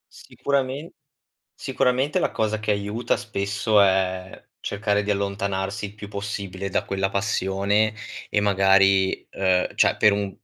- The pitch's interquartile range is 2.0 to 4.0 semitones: No, narrow, 1.6 semitones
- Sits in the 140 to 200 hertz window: No, low, 100 Hz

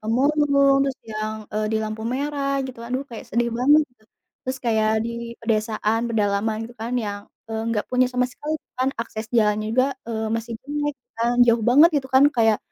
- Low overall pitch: No, high, 235 Hz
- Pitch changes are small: No, average, 3.4 semitones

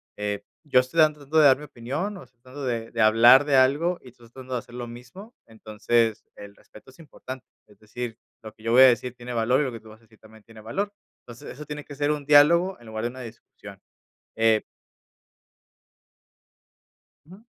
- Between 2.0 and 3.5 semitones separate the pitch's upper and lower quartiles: No, average, 4.4 semitones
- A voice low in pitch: Yes, low, 125 Hz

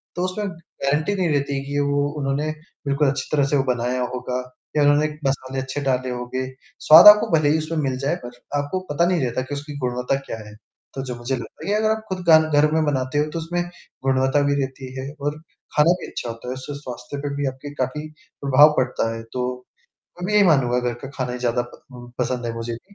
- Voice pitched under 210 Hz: Yes, medium, 140 Hz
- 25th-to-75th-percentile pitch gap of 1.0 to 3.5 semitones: Yes, average, 3.1 semitones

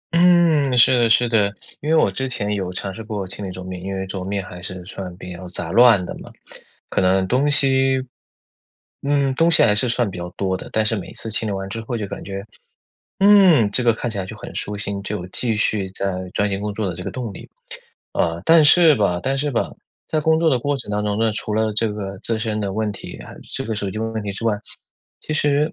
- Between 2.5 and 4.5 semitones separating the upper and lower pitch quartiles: No, average, 5.0 semitones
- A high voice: No, low, 105 Hz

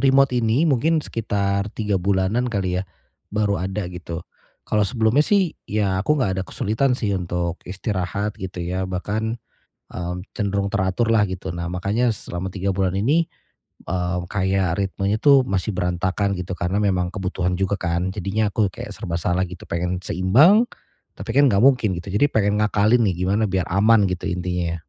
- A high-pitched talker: No, low, 100 Hz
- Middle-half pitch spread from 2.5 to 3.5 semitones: Yes, average, 3.2 semitones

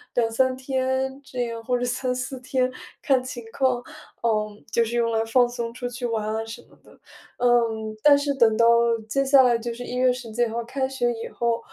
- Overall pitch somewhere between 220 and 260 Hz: Yes, high, 245 Hz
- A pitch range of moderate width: No, narrow, 2.0 semitones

